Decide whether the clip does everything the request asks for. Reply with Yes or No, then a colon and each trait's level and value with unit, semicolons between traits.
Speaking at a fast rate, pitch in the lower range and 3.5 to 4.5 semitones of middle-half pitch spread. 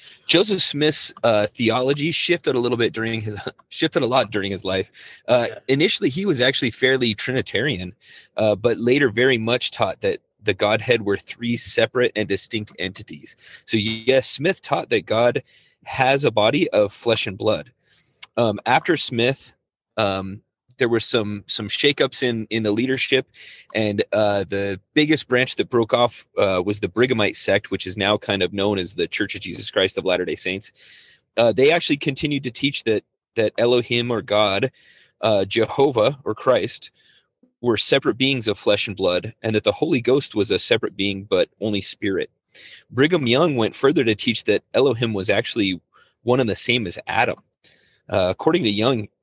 No: average, 180 wpm; low, 115 Hz; average, 4.1 semitones